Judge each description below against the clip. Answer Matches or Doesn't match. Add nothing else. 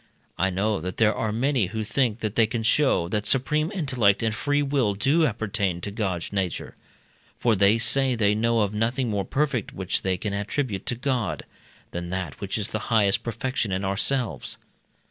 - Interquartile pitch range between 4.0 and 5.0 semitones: Matches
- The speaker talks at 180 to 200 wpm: Matches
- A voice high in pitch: Doesn't match